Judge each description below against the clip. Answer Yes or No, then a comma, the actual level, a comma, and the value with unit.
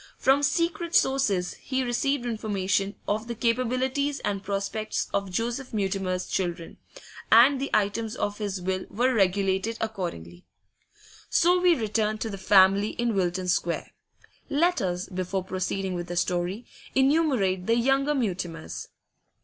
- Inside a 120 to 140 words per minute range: Yes, slow, 135 wpm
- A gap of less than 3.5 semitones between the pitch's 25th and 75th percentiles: No, average, 5.2 semitones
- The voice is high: Yes, high, 210 Hz